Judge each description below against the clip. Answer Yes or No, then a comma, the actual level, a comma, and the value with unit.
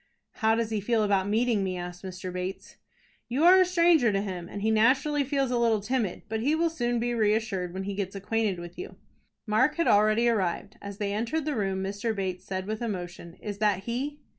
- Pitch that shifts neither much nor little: Yes, average, 3.9 semitones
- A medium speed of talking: No, fast, 215 wpm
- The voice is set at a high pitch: Yes, high, 215 Hz